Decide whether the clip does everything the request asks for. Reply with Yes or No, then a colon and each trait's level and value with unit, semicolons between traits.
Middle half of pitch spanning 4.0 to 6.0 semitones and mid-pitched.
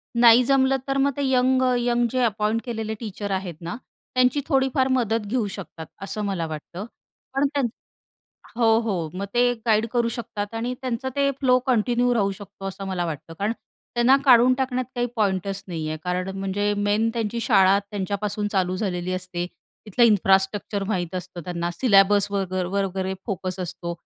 No: average, 4.3 semitones; high, 205 Hz